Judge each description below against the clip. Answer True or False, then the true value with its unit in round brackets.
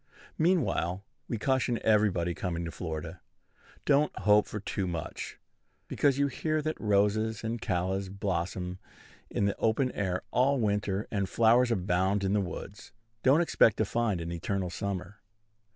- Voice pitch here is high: False (100 Hz)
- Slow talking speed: False (150 wpm)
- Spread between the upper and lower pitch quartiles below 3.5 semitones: False (4.1 semitones)